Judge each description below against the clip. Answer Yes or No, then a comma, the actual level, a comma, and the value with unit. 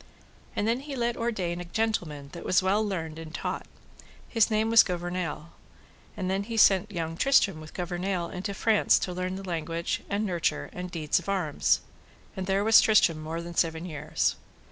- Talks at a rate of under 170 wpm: No, average, 185 wpm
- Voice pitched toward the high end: No, medium, 180 Hz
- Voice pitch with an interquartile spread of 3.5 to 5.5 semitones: Yes, average, 3.8 semitones